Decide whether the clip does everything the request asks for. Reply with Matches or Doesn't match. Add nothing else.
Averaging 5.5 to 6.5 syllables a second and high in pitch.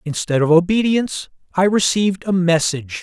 Doesn't match